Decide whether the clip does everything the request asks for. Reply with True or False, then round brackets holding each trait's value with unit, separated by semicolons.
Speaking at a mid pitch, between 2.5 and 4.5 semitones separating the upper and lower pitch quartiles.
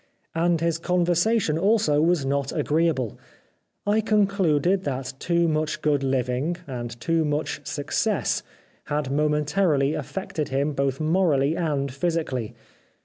True (155 Hz; 3.7 semitones)